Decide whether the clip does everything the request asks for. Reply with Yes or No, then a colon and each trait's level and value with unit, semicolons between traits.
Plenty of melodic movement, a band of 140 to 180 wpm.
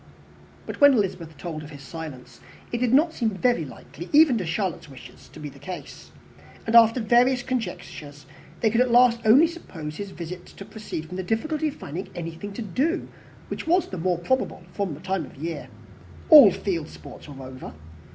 No: wide, 7.2 semitones; average, 190 wpm